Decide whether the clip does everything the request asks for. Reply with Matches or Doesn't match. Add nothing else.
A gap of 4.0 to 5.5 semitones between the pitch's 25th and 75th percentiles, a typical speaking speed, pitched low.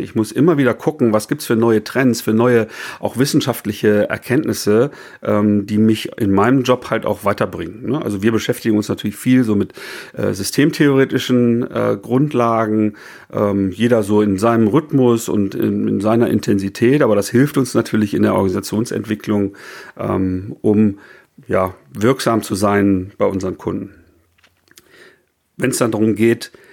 Doesn't match